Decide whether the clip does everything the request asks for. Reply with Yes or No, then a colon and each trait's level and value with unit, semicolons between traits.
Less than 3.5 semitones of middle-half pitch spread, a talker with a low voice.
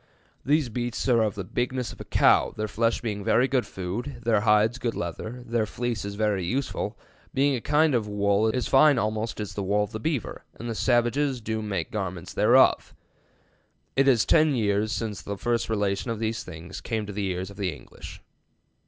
Yes: average, 3.1 semitones; low, 110 Hz